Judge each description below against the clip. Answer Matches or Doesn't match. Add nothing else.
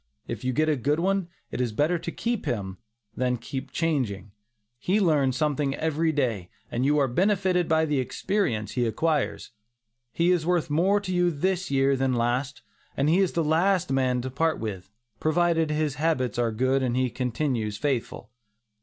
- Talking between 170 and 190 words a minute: Matches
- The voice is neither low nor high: Matches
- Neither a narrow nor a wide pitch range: Matches